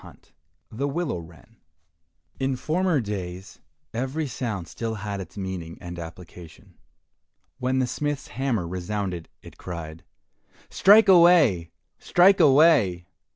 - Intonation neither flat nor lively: No, wide, 8.2 semitones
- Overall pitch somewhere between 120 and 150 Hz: No, low, 105 Hz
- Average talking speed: No, slow, 115 wpm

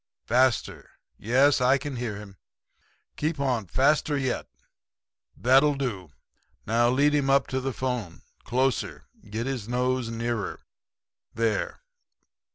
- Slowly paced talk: Yes, slow, 120 wpm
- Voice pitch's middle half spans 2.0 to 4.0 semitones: Yes, average, 2.9 semitones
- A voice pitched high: No, low, 125 Hz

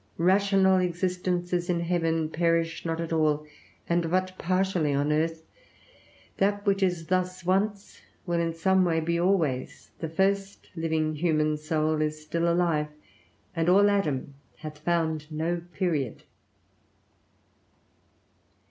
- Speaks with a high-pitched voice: No, medium, 170 Hz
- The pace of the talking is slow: Yes, slow, 125 wpm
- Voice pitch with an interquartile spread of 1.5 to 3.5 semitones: Yes, average, 2.7 semitones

